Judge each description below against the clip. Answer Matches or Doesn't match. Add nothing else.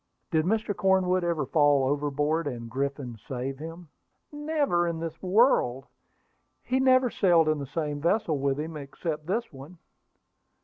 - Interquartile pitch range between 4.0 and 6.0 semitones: Matches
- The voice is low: Doesn't match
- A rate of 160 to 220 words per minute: Doesn't match